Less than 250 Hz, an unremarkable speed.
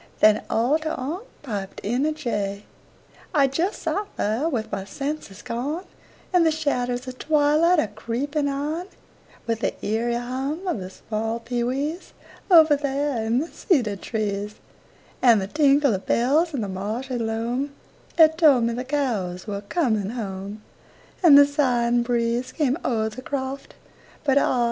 No: very high, 255 Hz; average, 160 wpm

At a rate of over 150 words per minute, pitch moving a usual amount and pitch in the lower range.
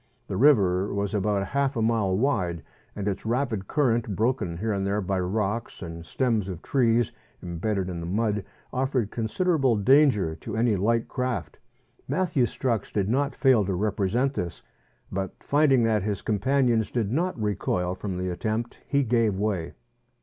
Yes: average, 165 wpm; average, 4.4 semitones; low, 110 Hz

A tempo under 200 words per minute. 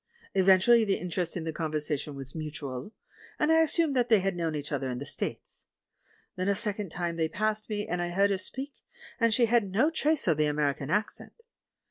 No: fast, 205 wpm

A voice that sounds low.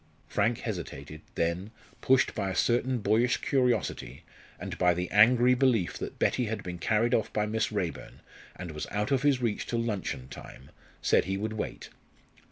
Yes: low, 105 Hz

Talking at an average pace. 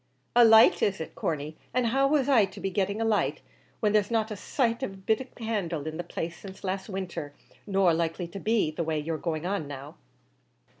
No: fast, 230 wpm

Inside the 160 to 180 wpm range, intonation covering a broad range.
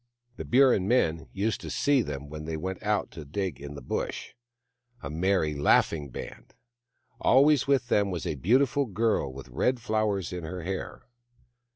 Yes: average, 170 wpm; wide, 7.0 semitones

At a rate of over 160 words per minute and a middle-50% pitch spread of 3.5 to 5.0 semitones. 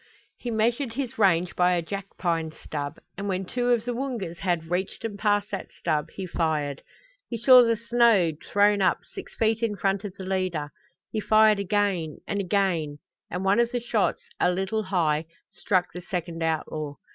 Yes: average, 180 wpm; average, 4.3 semitones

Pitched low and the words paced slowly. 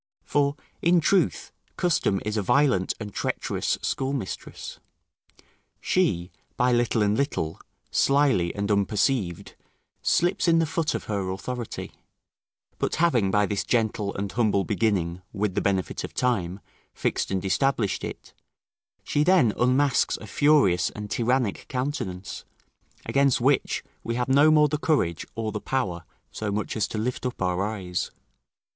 No: low, 110 Hz; average, 145 wpm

